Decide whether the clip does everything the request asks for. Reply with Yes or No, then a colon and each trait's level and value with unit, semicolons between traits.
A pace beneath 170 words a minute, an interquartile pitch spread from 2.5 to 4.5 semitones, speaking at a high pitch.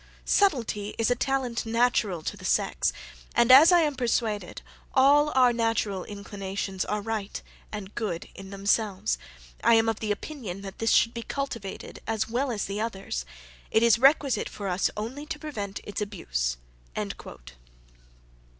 Yes: average, 150 wpm; average, 3.8 semitones; high, 225 Hz